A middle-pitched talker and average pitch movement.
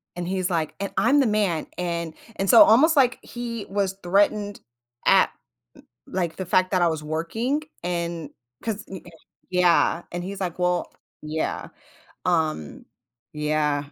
Yes: medium, 180 Hz; average, 3.5 semitones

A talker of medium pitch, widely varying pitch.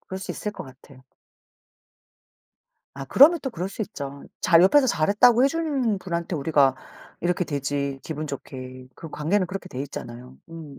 Yes: medium, 165 Hz; wide, 6.6 semitones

